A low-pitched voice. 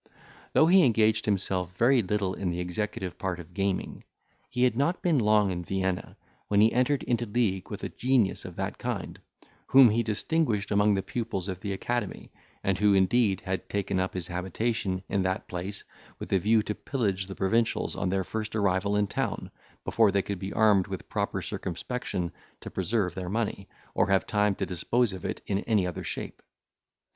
Yes: low, 100 Hz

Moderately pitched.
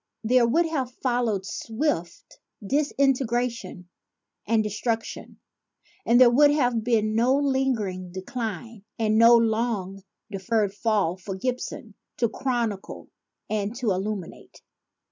No: high, 230 Hz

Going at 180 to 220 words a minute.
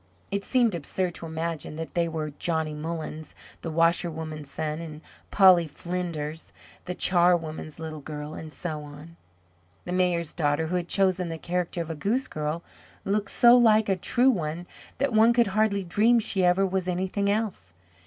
No: average, 170 wpm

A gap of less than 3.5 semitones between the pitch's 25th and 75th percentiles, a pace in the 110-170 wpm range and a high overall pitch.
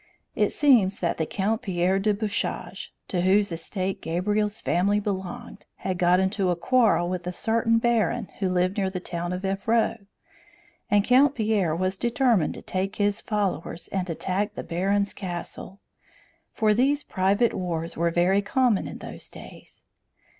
Yes: average, 3.0 semitones; average, 160 wpm; high, 195 Hz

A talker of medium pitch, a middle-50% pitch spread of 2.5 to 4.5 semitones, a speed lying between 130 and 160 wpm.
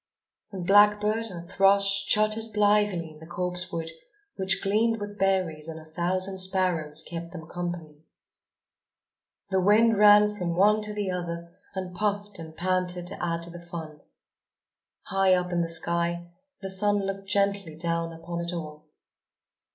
Yes: medium, 180 Hz; average, 2.9 semitones; average, 150 wpm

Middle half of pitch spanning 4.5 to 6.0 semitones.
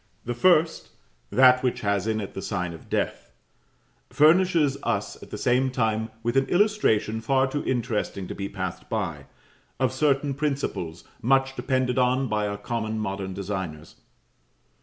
Yes: average, 4.9 semitones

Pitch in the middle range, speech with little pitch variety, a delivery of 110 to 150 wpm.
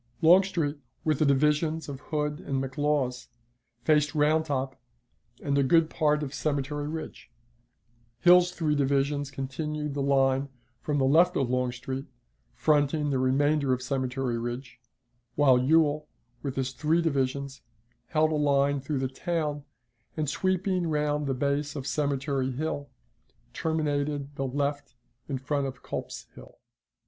Yes: medium, 145 Hz; narrow, 2.2 semitones; average, 140 wpm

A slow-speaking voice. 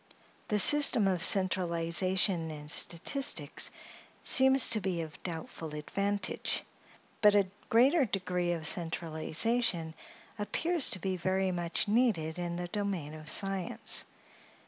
Yes: slow, 120 wpm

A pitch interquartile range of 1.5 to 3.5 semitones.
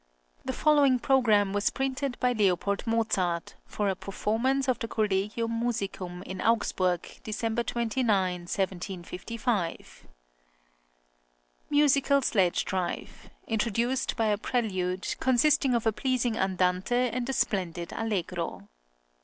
No: average, 4.6 semitones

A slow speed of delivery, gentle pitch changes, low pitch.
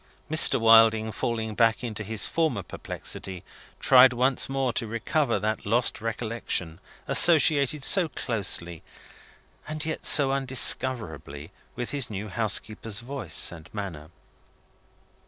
No: slow, 120 wpm; average, 4.5 semitones; low, 115 Hz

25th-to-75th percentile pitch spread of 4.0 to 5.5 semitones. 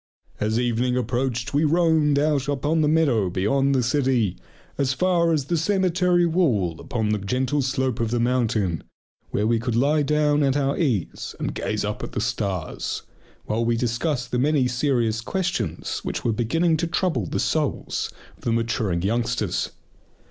Yes: average, 4.9 semitones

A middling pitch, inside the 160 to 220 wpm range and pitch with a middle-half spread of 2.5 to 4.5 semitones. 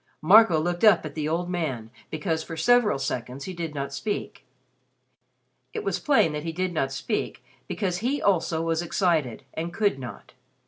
Yes: medium, 165 Hz; average, 175 wpm; average, 3.9 semitones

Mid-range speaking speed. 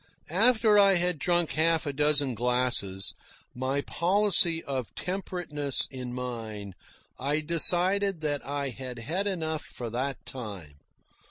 No: slow, 125 wpm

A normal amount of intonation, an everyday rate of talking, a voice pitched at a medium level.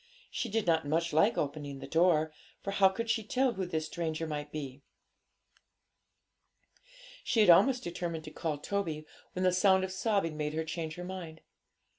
Yes: average, 3.7 semitones; average, 175 wpm; medium, 170 Hz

